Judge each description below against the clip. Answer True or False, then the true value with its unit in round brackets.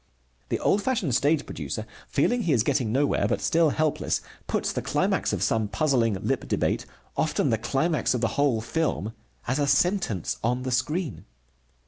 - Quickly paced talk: False (170 wpm)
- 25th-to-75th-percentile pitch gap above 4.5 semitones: True (5.3 semitones)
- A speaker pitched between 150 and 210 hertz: False (140 Hz)